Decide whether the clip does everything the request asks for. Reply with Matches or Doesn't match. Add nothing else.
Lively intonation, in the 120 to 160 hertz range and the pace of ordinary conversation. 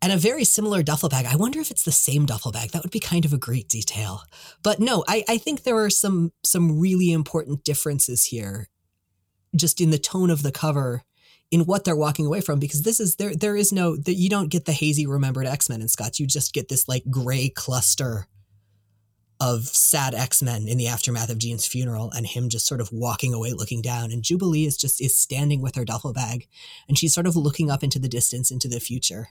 Doesn't match